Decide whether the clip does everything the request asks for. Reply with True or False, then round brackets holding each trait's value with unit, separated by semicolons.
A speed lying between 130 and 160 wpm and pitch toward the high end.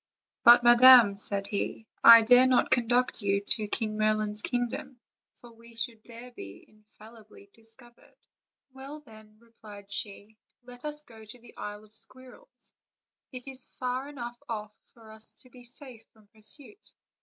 True (155 wpm; 230 Hz)